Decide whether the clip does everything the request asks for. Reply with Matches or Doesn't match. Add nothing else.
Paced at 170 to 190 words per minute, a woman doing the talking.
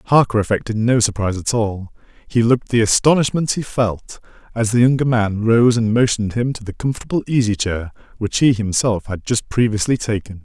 Doesn't match